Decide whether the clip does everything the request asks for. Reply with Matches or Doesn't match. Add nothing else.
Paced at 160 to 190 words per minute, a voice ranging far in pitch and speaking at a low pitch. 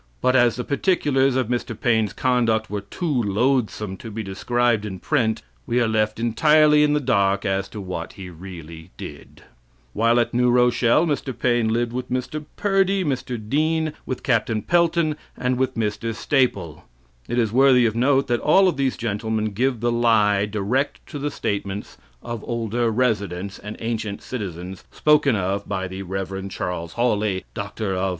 Doesn't match